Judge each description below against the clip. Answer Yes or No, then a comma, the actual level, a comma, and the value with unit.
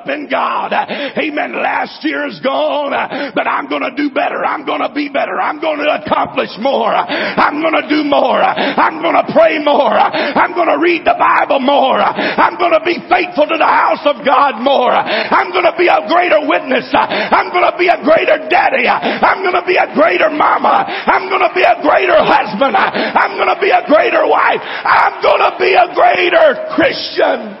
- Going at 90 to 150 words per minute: No, average, 175 wpm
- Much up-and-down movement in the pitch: No, average, 2.9 semitones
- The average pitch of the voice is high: Yes, very high, 325 Hz